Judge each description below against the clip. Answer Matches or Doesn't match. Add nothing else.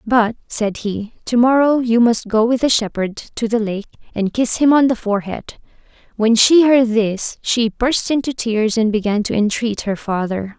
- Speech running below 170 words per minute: Doesn't match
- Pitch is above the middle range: Matches